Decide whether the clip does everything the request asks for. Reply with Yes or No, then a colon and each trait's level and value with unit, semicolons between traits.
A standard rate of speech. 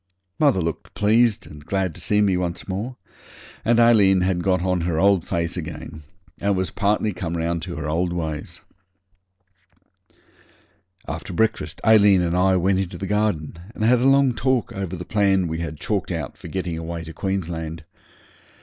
Yes: average, 175 wpm